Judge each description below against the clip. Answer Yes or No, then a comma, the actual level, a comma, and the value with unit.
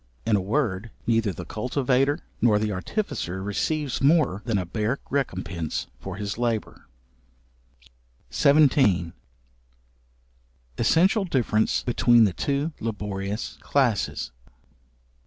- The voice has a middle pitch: No, low, 115 Hz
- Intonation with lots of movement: Yes, wide, 5.9 semitones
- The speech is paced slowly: Yes, slow, 100 wpm